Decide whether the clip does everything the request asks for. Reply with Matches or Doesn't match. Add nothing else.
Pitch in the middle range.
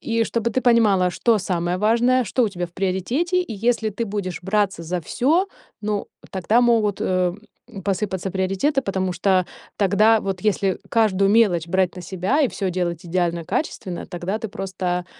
Doesn't match